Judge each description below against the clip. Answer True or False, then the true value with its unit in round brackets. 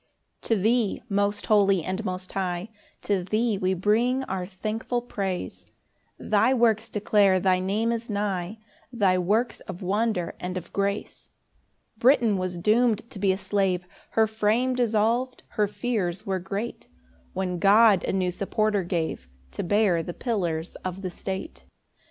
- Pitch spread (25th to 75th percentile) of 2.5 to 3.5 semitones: True (3.2 semitones)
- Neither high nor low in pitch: False (200 Hz)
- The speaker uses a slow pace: False (155 wpm)